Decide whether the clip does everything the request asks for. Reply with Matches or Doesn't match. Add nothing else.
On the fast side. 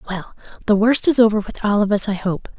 Matches